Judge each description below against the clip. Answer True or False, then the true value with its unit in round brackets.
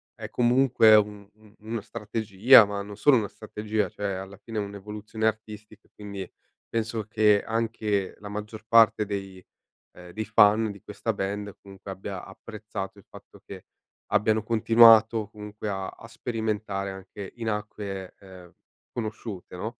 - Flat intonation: True (1.7 semitones)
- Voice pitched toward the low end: True (105 Hz)